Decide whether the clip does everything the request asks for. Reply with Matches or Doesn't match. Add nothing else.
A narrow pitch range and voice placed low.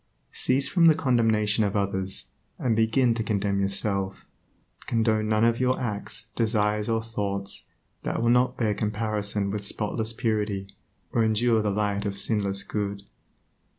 Matches